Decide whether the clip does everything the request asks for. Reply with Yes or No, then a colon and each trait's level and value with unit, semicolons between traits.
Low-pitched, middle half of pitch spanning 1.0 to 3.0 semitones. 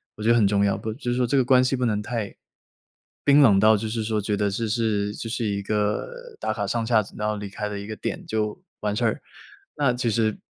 Yes: low, 110 Hz; narrow, 2.6 semitones